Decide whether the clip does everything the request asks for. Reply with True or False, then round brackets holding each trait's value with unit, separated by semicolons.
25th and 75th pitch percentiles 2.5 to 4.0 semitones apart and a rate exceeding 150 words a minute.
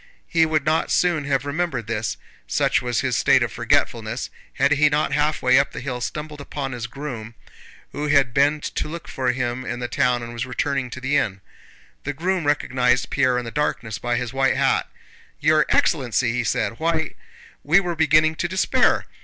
True (3.7 semitones; 190 wpm)